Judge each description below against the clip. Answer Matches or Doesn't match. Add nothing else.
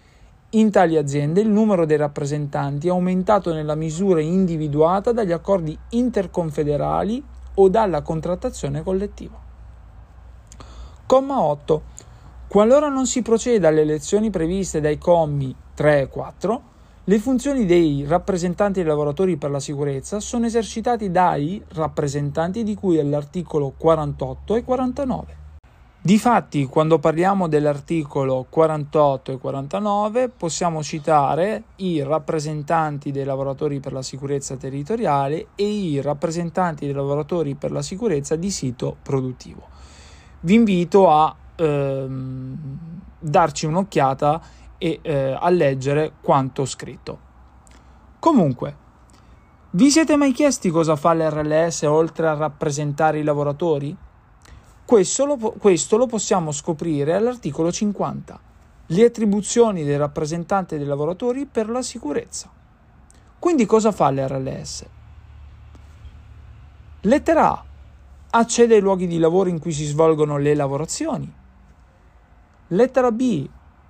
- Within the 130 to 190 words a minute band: Doesn't match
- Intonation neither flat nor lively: Doesn't match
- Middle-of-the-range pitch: Matches